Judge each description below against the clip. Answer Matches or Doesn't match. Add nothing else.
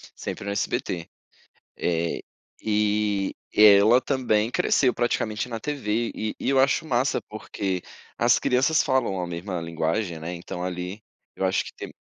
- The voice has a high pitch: Doesn't match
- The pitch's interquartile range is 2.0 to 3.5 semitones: Doesn't match